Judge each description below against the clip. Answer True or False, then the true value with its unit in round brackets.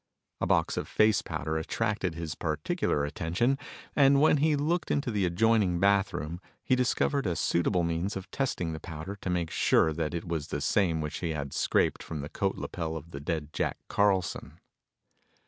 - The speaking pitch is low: True (90 Hz)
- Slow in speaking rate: False (180 wpm)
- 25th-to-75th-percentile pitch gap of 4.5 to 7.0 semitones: True (5.0 semitones)